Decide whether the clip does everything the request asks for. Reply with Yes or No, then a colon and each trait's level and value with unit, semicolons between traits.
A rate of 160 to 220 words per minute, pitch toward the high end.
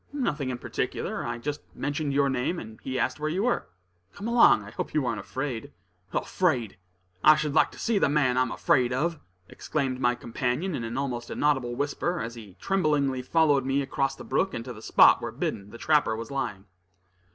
No: average, 200 wpm; low, 135 Hz